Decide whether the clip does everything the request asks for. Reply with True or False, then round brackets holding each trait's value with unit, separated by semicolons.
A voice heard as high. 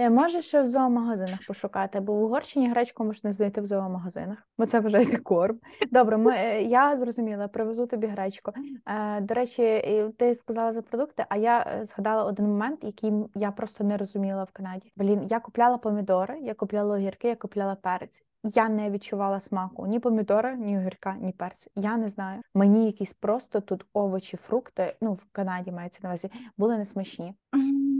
True (215 Hz)